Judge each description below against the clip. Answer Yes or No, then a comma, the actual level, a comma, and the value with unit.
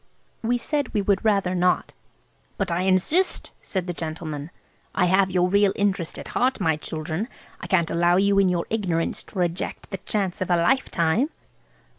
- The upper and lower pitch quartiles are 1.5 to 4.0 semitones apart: Yes, average, 2.8 semitones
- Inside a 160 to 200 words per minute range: Yes, average, 170 wpm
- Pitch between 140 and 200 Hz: Yes, medium, 185 Hz